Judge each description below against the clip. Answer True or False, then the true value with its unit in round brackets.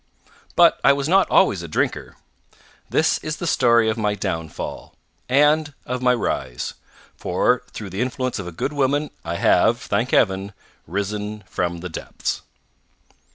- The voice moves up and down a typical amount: False (6.2 semitones)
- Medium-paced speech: True (155 wpm)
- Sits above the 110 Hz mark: False (105 Hz)